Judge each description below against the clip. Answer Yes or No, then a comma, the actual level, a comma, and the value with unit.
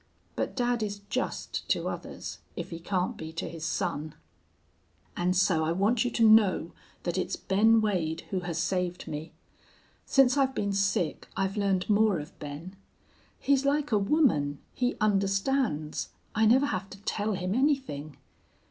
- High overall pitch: Yes, high, 195 Hz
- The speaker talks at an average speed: Yes, average, 160 wpm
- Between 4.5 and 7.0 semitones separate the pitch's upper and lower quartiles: Yes, average, 5.0 semitones